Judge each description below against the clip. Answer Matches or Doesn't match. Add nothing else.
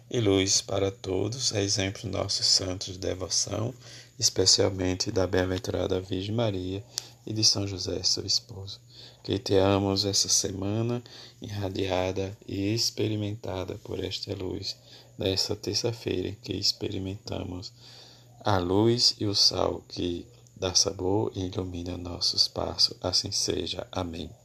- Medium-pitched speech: Doesn't match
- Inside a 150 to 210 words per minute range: Doesn't match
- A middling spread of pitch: Matches